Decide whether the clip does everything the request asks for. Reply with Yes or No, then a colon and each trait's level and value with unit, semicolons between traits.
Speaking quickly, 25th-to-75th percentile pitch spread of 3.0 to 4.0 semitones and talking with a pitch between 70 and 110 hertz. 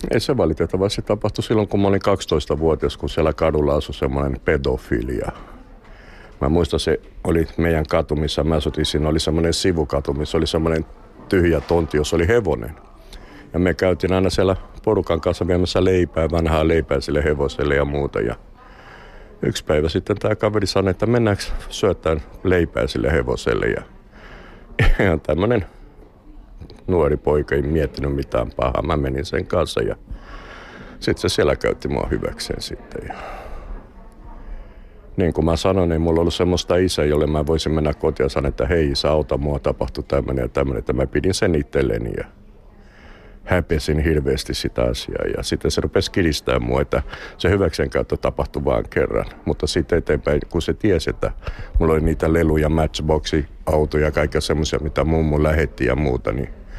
Yes: fast, 165 wpm; average, 3.7 semitones; very low, 80 Hz